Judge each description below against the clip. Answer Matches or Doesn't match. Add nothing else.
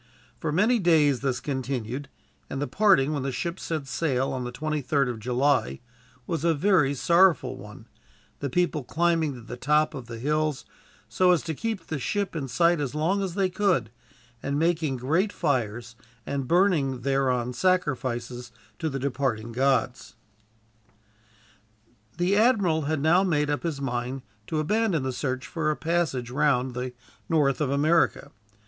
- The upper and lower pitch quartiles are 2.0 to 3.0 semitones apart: Doesn't match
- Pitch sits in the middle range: Matches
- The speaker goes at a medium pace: Matches